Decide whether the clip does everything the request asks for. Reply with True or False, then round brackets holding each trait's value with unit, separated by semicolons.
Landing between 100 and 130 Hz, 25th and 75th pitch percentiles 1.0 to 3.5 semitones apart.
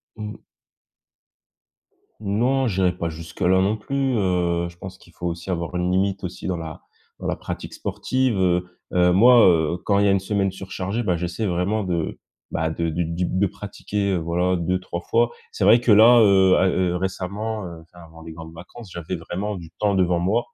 False (90 Hz; 2.9 semitones)